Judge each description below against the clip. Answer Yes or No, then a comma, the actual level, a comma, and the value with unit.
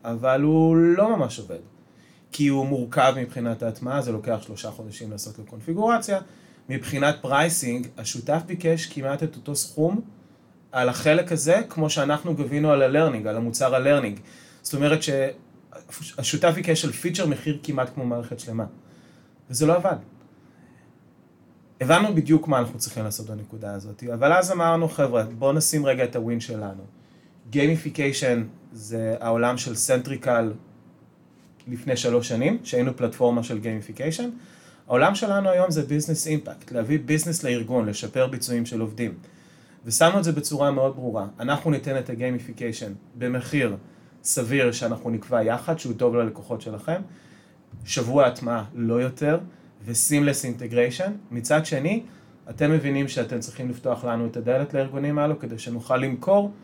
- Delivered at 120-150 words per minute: Yes, average, 140 wpm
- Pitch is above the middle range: No, low, 130 Hz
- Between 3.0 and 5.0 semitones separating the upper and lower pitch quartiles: Yes, average, 4.7 semitones